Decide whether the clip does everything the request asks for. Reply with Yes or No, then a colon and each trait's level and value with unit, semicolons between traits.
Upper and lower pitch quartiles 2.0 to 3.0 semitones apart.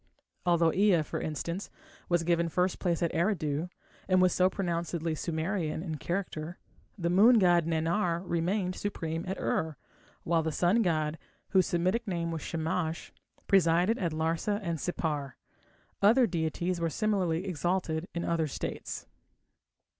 Yes: narrow, 2.4 semitones